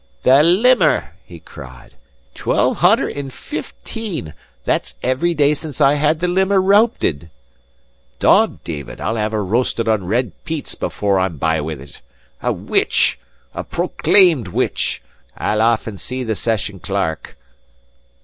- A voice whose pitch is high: No, low, 115 Hz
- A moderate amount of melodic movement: No, wide, 8.9 semitones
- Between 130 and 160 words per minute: Yes, average, 140 wpm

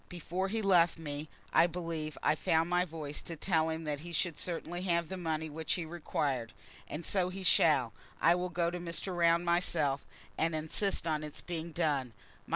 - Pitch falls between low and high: Yes, medium, 165 Hz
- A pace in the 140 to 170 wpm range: No, average, 190 wpm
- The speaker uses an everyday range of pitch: No, narrow, 2.3 semitones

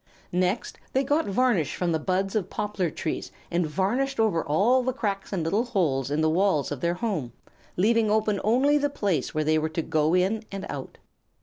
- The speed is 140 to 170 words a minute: No, average, 200 wpm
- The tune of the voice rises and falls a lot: Yes, wide, 5.7 semitones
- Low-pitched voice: No, high, 195 Hz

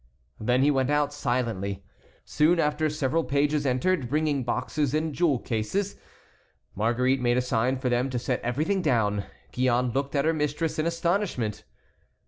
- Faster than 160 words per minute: No, average, 155 wpm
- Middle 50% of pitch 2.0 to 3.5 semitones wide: No, average, 4.0 semitones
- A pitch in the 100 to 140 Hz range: Yes, low, 135 Hz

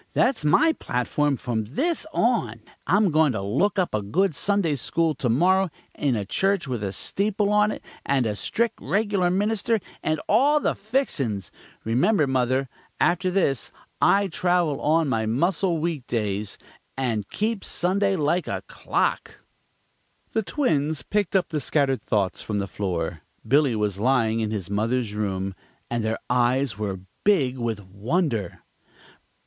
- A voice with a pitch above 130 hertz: Yes, medium, 140 Hz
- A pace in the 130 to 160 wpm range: Yes, average, 150 wpm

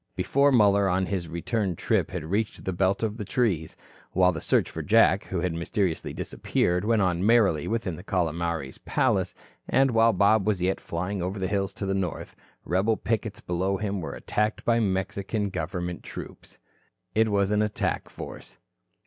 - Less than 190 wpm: Yes, average, 175 wpm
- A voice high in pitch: No, very low, 95 Hz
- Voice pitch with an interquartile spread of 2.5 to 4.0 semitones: Yes, average, 3.1 semitones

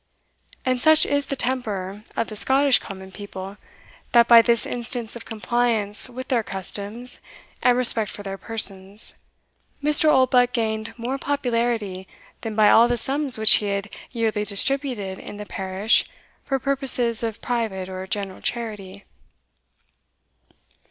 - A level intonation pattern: No, average, 3.5 semitones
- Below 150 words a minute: Yes, average, 140 wpm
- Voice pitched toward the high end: Yes, high, 225 Hz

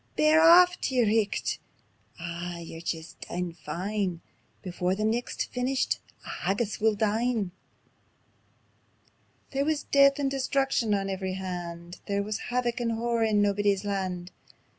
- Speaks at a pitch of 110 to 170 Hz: No, high, 205 Hz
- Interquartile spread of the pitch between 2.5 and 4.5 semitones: No, average, 5.3 semitones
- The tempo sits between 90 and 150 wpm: Yes, average, 140 wpm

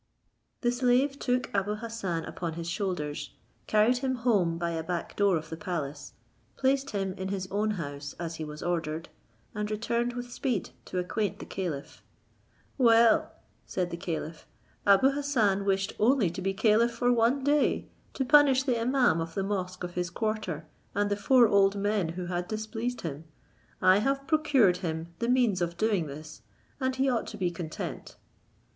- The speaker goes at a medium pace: Yes, average, 175 wpm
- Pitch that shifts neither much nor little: No, wide, 5.7 semitones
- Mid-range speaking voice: No, high, 200 Hz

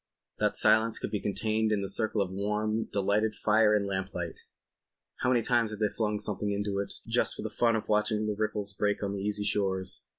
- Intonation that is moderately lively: No, narrow, 1.3 semitones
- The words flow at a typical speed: No, fast, 210 wpm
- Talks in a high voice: No, low, 105 Hz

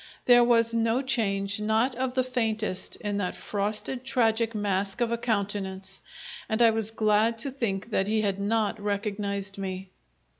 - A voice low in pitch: No, high, 215 Hz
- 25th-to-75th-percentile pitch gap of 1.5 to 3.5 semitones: Yes, narrow, 2.6 semitones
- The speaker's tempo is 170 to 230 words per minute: No, average, 160 wpm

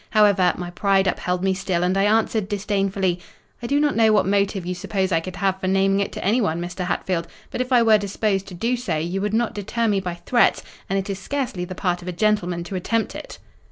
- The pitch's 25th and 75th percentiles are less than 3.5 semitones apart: Yes, average, 2.8 semitones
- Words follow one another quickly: Yes, fast, 240 wpm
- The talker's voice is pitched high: Yes, high, 195 Hz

